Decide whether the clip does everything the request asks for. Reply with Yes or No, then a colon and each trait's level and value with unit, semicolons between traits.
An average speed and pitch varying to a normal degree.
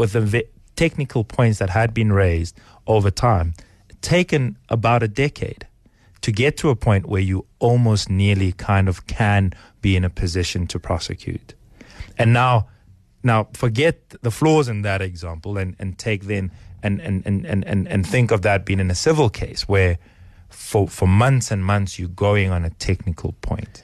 Yes: average, 180 wpm; average, 3.6 semitones